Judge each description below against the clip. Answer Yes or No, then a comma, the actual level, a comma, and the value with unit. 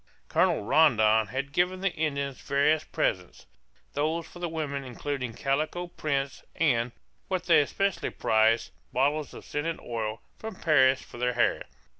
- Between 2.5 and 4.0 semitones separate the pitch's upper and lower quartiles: No, average, 4.4 semitones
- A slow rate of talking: No, average, 145 wpm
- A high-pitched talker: No, medium, 140 Hz